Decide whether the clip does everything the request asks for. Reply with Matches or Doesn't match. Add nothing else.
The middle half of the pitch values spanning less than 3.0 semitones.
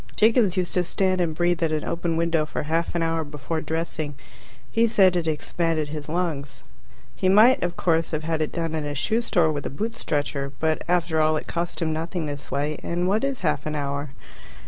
Matches